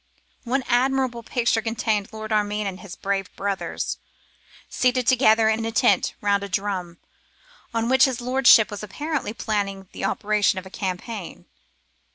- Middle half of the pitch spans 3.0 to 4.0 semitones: Yes, average, 3.3 semitones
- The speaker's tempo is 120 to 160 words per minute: Yes, average, 150 wpm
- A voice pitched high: Yes, high, 215 Hz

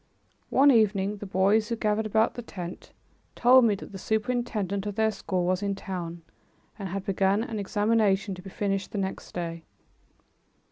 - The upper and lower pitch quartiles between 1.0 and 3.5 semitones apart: Yes, narrow, 2.4 semitones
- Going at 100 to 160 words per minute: No, average, 175 wpm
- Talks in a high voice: Yes, high, 200 Hz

